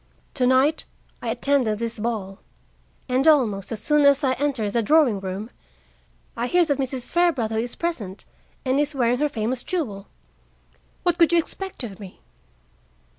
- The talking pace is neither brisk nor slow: Yes, average, 155 wpm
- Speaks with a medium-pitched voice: No, very high, 255 Hz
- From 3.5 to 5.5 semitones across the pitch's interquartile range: Yes, average, 5.2 semitones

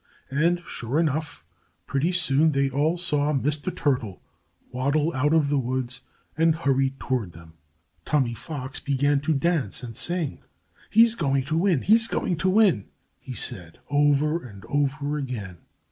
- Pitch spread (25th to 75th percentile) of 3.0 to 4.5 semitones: Yes, average, 3.7 semitones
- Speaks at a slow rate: No, average, 150 wpm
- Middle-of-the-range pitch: Yes, medium, 145 Hz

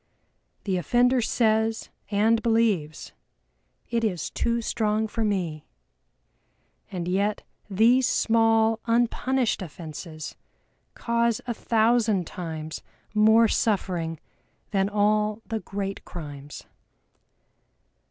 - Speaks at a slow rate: Yes, slow, 95 wpm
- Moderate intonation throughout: Yes, average, 3.9 semitones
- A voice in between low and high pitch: No, high, 215 Hz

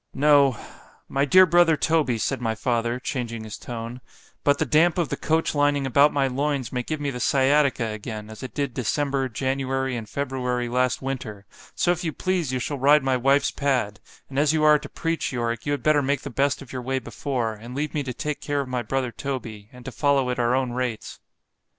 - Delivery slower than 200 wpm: No, fast, 205 wpm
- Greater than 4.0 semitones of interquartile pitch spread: No, average, 2.9 semitones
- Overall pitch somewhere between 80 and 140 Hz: Yes, low, 135 Hz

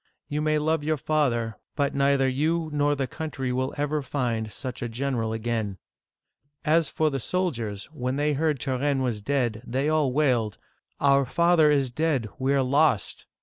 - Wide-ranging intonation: No, average, 3.5 semitones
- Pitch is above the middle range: No, medium, 140 Hz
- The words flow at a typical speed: Yes, average, 175 wpm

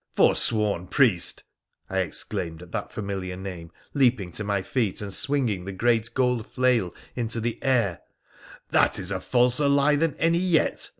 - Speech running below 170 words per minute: No, average, 175 wpm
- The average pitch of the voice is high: No, low, 110 Hz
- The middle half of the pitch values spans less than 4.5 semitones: No, average, 5.2 semitones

